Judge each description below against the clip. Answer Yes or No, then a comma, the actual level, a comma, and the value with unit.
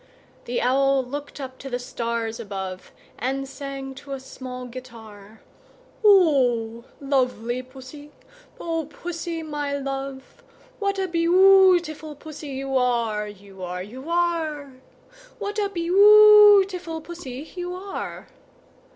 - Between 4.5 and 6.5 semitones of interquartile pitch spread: Yes, wide, 5.4 semitones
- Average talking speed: No, slow, 115 wpm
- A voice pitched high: Yes, very high, 275 Hz